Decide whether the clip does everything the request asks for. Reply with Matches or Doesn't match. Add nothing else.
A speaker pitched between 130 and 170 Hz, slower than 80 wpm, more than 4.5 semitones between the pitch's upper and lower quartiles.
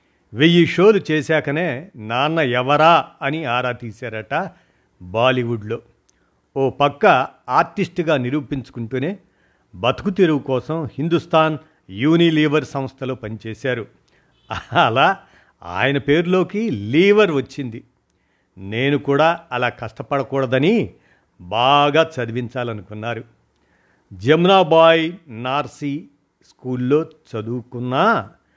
Matches